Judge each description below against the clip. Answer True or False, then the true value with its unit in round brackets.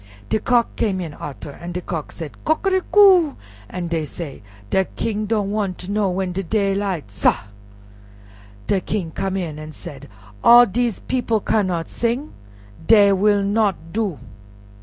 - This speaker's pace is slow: False (155 wpm)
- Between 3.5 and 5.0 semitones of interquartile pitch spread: True (4.5 semitones)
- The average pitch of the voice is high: True (195 Hz)